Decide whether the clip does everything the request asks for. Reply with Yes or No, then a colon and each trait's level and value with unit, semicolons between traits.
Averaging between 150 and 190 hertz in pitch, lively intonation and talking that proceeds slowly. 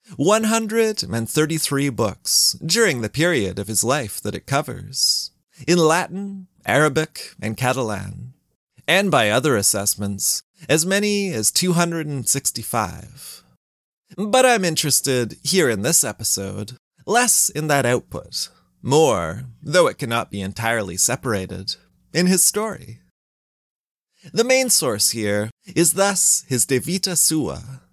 No: medium, 140 Hz; wide, 8.3 semitones; slow, 120 wpm